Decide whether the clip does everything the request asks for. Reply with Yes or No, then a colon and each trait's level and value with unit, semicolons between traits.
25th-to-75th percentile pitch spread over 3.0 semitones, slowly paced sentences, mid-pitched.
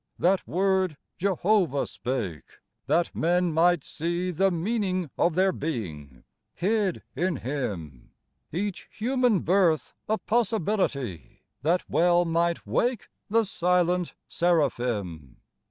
Yes: average, 5.2 semitones; slow, 105 wpm; medium, 175 Hz